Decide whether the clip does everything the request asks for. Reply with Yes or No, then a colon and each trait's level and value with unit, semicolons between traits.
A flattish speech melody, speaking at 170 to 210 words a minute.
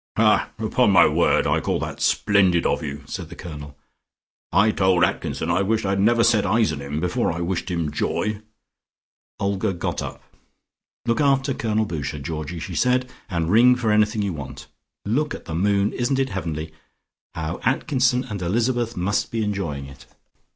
No: wide, 5.6 semitones; average, 180 wpm